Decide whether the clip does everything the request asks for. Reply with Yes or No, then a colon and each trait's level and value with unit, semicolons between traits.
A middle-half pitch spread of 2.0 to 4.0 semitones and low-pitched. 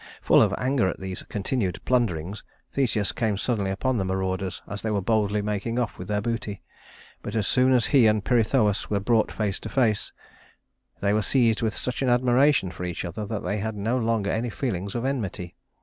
Yes: average, 3.6 semitones; low, 110 Hz